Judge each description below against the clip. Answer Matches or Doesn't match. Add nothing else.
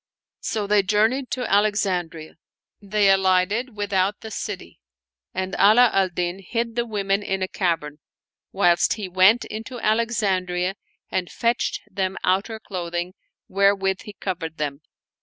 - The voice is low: Doesn't match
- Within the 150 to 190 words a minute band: Doesn't match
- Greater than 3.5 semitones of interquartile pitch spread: Doesn't match